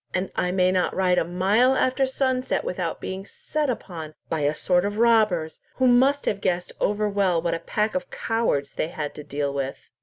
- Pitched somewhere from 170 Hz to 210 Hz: Yes, high, 190 Hz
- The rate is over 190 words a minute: Yes, fast, 205 wpm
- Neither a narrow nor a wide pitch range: No, wide, 5.7 semitones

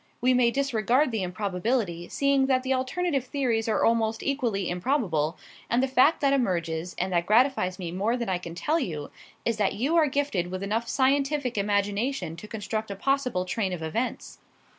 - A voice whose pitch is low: No, high, 225 Hz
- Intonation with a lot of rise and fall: Yes, wide, 6.1 semitones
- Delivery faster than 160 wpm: Yes, average, 185 wpm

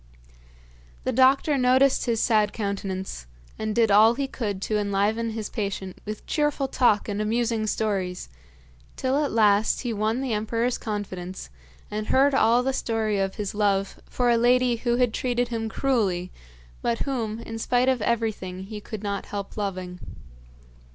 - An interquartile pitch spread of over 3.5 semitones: No, average, 3.2 semitones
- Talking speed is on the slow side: No, average, 160 wpm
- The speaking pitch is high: Yes, high, 220 Hz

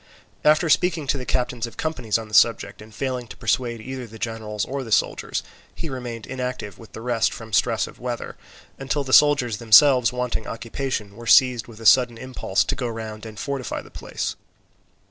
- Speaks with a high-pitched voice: No, low, 120 Hz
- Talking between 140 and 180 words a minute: No, average, 195 wpm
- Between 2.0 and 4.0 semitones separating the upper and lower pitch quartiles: Yes, average, 2.7 semitones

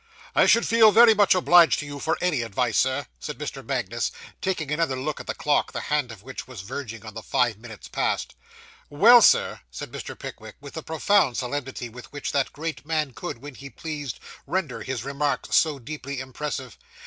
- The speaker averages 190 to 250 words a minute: Yes, average, 195 wpm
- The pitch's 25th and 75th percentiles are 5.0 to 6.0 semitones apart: No, average, 4.1 semitones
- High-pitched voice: No, medium, 140 Hz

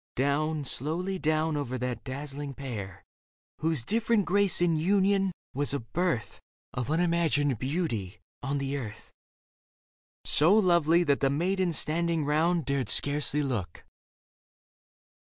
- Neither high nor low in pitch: Yes, medium, 150 Hz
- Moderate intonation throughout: Yes, average, 4.0 semitones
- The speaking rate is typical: No, slow, 120 wpm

